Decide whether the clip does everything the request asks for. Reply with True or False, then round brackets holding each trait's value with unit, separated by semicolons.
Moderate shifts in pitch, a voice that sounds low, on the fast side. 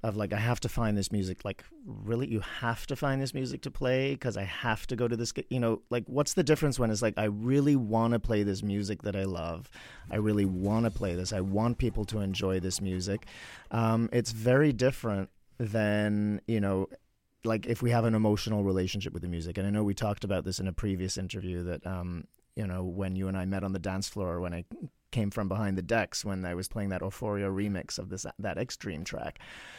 True (3.4 semitones; 105 Hz; 235 wpm)